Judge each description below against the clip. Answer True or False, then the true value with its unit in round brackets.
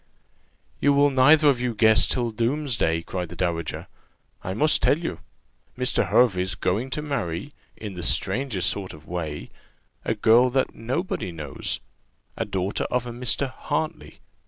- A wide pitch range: True (6.7 semitones)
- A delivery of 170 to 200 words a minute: False (155 wpm)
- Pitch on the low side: True (115 Hz)